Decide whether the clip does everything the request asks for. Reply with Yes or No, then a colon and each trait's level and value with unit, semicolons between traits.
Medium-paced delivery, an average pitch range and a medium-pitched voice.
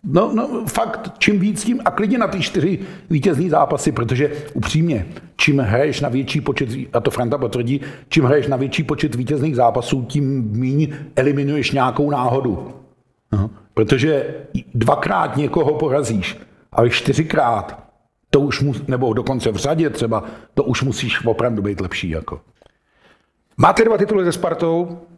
Yes: average, 155 wpm; average, 4.5 semitones; medium, 145 Hz